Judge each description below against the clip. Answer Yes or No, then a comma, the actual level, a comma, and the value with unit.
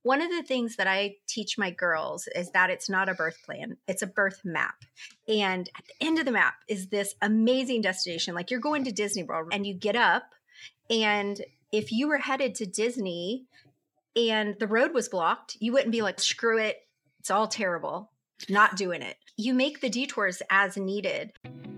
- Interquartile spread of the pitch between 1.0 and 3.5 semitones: No, average, 4.5 semitones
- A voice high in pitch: Yes, high, 215 Hz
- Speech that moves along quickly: No, average, 195 wpm